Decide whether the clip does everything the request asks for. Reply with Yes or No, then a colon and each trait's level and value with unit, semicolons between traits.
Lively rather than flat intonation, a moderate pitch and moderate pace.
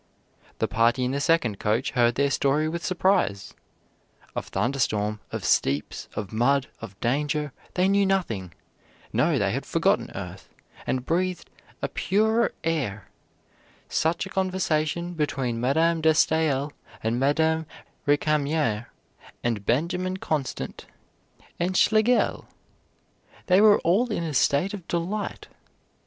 No: wide, 6.4 semitones; medium, 150 Hz; slow, 130 wpm